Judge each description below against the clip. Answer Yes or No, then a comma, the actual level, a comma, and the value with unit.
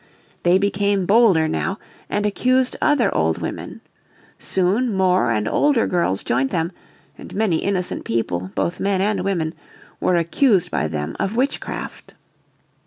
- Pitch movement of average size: Yes, average, 4.6 semitones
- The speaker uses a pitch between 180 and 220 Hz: Yes, medium, 185 Hz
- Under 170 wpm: Yes, average, 140 wpm